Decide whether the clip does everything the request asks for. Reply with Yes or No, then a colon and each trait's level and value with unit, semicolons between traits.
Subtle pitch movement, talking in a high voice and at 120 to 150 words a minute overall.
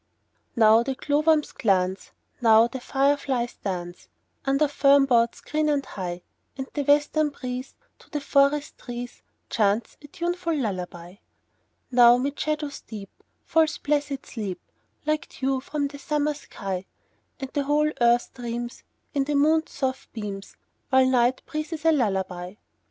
No: average, 4.5 semitones; very high, 265 Hz; average, 140 wpm